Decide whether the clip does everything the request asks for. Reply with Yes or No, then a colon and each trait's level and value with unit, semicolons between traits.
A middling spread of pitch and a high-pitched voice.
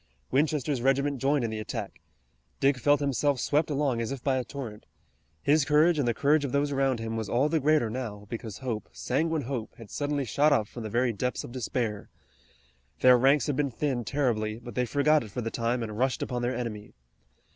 No: average, 3.7 semitones; low, 130 Hz